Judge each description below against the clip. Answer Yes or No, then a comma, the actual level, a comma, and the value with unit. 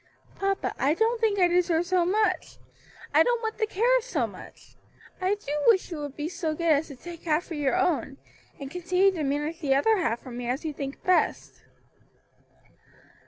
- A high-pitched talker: Yes, very high, 340 Hz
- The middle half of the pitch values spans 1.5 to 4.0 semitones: No, average, 5.0 semitones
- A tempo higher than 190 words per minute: Yes, average, 200 wpm